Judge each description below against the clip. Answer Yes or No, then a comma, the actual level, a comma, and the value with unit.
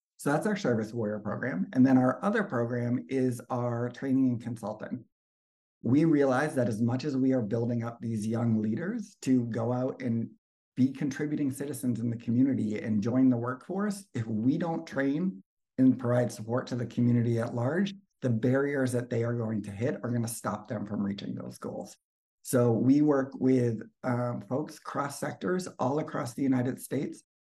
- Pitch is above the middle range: No, low, 125 Hz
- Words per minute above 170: Yes, average, 185 wpm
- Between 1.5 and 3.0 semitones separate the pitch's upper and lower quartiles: Yes, narrow, 2.6 semitones